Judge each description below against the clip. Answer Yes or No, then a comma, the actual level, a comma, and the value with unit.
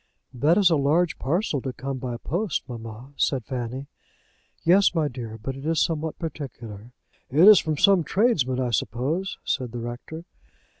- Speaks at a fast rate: No, average, 160 wpm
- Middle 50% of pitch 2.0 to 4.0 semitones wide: No, average, 5.1 semitones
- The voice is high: No, medium, 140 Hz